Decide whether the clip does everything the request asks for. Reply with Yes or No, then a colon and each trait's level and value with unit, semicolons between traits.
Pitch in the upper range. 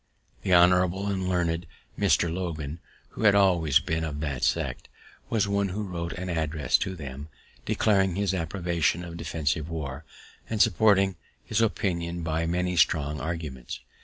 No: very low, 85 Hz